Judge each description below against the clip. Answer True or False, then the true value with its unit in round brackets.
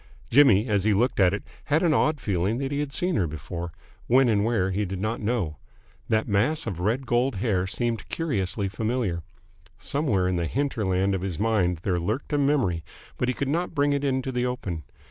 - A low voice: True (110 Hz)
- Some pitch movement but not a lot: False (6.0 semitones)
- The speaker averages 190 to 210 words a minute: True (205 wpm)